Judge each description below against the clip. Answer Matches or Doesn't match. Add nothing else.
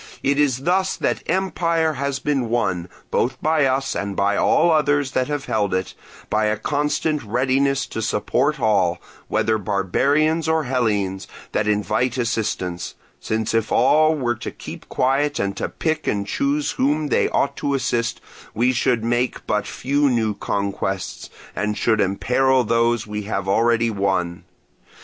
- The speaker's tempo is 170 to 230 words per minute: Doesn't match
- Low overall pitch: Matches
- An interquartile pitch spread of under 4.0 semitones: Doesn't match